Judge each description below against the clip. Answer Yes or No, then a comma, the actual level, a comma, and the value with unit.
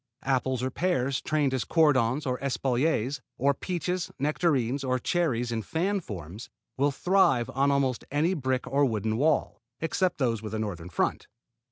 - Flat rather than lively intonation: No, average, 4.3 semitones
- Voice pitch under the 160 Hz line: Yes, low, 135 Hz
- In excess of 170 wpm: No, average, 160 wpm